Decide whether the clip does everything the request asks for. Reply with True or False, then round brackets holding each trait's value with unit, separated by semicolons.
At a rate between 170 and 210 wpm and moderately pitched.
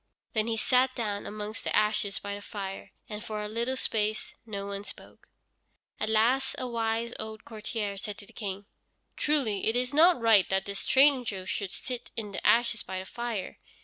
False (190 wpm; 215 Hz)